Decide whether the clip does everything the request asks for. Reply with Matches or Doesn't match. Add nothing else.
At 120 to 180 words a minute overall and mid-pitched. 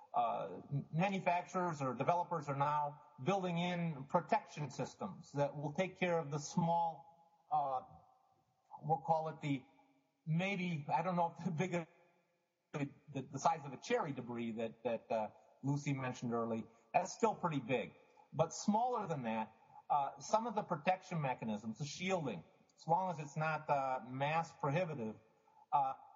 Matches